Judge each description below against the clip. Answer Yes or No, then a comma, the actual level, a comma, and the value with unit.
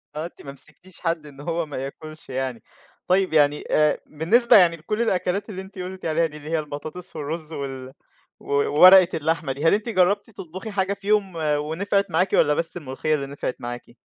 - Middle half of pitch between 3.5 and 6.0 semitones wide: Yes, average, 4.2 semitones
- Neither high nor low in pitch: Yes, medium, 165 Hz